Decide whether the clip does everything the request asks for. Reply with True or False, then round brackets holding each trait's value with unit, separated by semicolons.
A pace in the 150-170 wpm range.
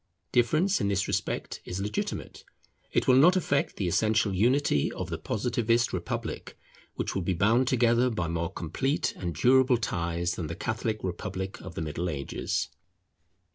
True (160 wpm)